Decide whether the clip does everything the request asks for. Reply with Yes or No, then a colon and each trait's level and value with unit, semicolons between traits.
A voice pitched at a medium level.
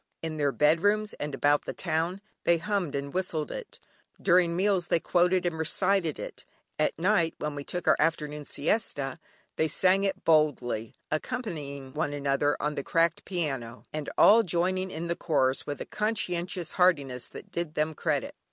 Yes: medium, 160 Hz